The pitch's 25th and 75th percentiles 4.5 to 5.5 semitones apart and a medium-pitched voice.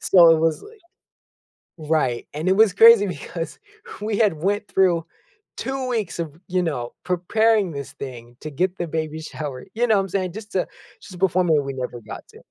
Yes: average, 5.1 semitones; medium, 180 Hz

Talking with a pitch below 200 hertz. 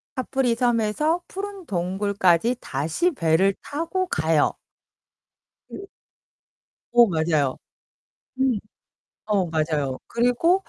No: high, 210 Hz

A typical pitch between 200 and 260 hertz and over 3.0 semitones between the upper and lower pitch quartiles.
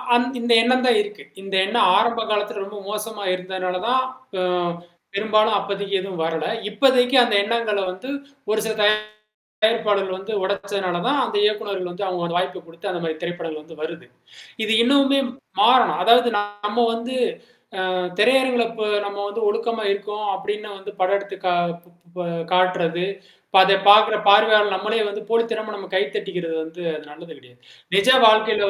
Yes: high, 205 Hz; average, 3.4 semitones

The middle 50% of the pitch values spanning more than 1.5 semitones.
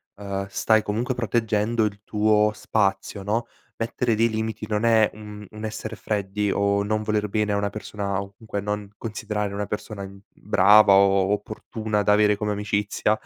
No: narrow, 1.2 semitones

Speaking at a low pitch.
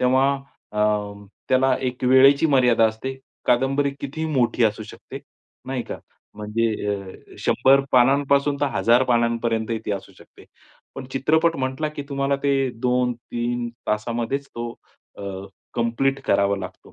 Yes: low, 125 Hz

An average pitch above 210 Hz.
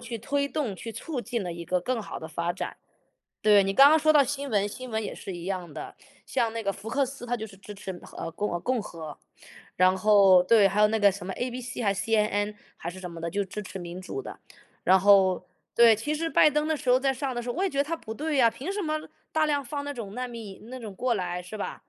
Yes: high, 220 Hz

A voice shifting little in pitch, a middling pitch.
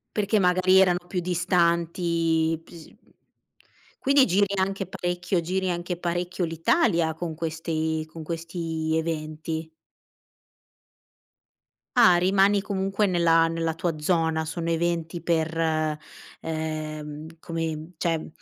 Yes: narrow, 2.0 semitones; medium, 170 Hz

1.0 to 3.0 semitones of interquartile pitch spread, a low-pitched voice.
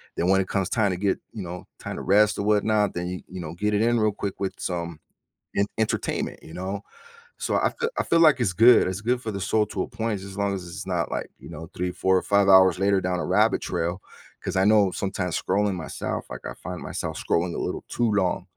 Yes: narrow, 2.6 semitones; very low, 95 Hz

